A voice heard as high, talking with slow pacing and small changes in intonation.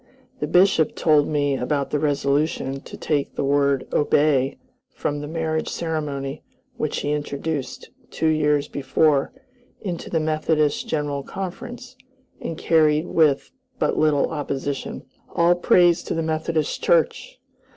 No: medium, 150 Hz; slow, 130 wpm; narrow, 2.2 semitones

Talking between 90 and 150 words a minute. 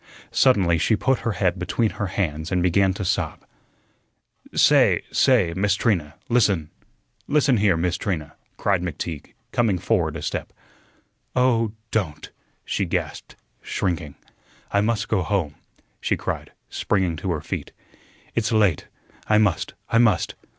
Yes: average, 140 wpm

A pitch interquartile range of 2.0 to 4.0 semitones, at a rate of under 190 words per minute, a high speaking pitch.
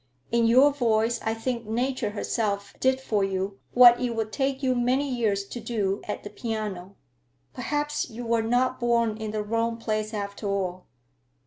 Yes: average, 2.8 semitones; average, 175 wpm; high, 230 Hz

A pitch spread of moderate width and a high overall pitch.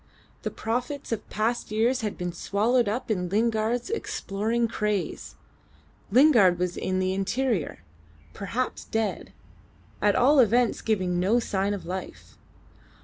Yes: average, 3.9 semitones; high, 215 Hz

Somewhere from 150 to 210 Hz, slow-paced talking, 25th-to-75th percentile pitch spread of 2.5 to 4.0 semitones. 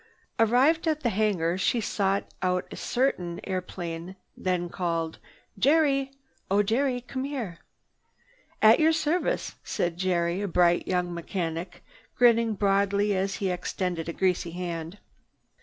No: high, 190 Hz; slow, 130 wpm; average, 5.1 semitones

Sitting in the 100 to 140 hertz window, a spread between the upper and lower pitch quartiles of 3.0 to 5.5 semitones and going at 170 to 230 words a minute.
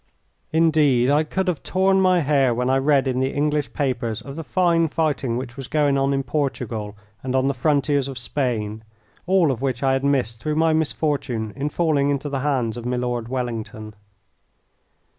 Yes: low, 135 Hz; average, 3.4 semitones; average, 185 wpm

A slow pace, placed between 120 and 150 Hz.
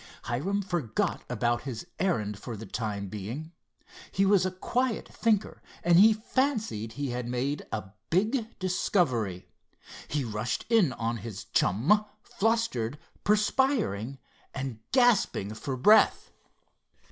Yes: slow, 125 wpm; medium, 140 Hz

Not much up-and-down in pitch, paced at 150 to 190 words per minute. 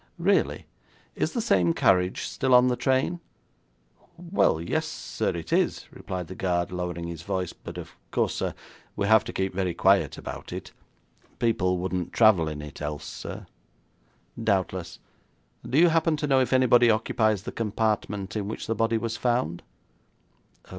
No: average, 5.1 semitones; average, 160 wpm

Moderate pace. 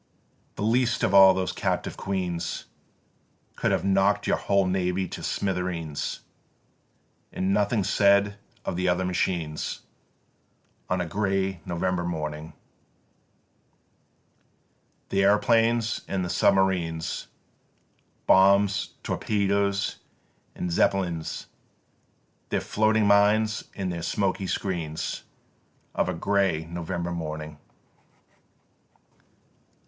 No: slow, 100 wpm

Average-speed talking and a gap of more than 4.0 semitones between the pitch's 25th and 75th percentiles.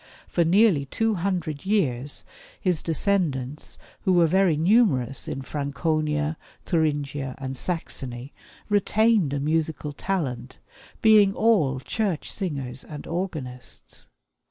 No: slow, 110 wpm; wide, 5.6 semitones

